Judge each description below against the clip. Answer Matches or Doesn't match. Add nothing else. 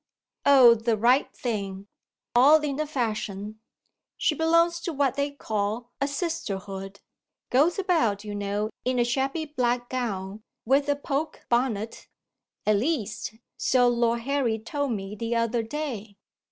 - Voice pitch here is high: Matches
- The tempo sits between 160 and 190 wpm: Doesn't match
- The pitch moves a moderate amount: Matches